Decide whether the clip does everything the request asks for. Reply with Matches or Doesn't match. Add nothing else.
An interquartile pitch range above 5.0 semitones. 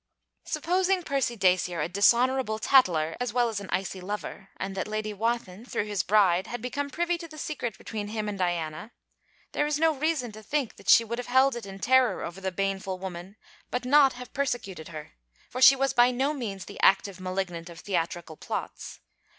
Matches